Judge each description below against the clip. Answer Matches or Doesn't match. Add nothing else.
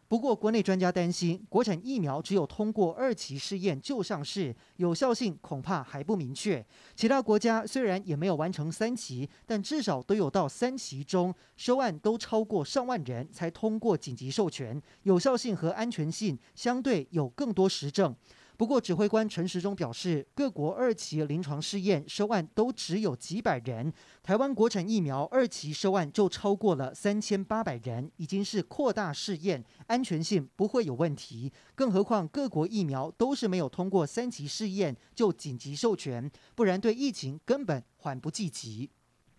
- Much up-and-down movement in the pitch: Matches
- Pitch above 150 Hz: Matches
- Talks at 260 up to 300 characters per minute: Matches